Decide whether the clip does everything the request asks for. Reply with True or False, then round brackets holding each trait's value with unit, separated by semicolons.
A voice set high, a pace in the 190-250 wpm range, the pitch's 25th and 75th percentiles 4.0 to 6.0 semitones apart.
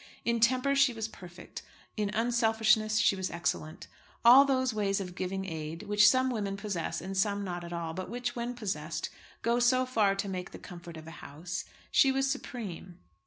True (205 Hz; 195 wpm; 5.1 semitones)